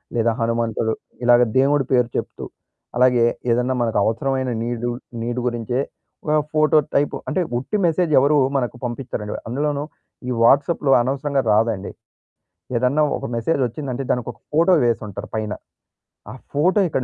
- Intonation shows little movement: No, average, 3.4 semitones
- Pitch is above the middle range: No, low, 125 Hz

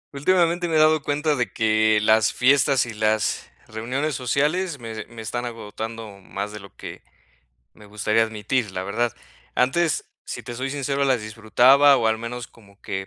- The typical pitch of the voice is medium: No, low, 115 Hz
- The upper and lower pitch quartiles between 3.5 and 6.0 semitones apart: Yes, average, 4.4 semitones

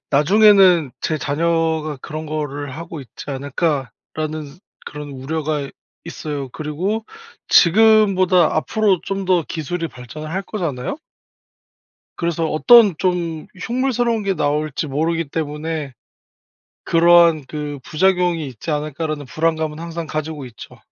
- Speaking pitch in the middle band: Yes, medium, 160 Hz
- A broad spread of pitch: No, average, 3.1 semitones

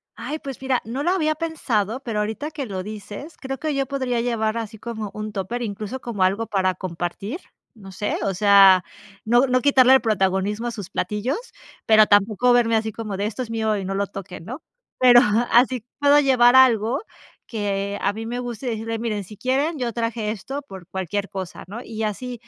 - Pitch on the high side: Yes, high, 225 Hz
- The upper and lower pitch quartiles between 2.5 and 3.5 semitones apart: No, average, 3.9 semitones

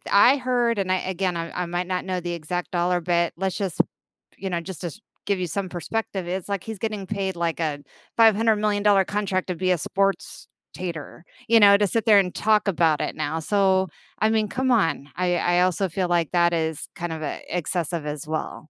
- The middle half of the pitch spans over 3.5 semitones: No, average, 3.1 semitones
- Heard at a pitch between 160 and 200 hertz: Yes, medium, 185 Hz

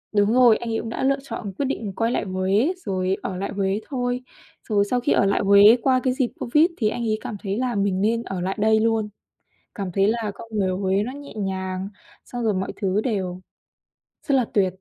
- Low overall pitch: No, high, 210 Hz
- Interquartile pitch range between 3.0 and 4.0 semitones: Yes, average, 3.7 semitones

